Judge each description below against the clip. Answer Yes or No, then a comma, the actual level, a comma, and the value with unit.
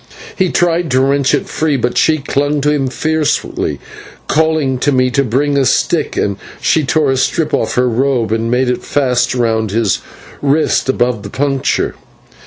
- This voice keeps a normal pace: Yes, average, 180 wpm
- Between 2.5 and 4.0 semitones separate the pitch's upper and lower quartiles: Yes, average, 3.1 semitones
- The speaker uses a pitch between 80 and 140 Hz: Yes, low, 135 Hz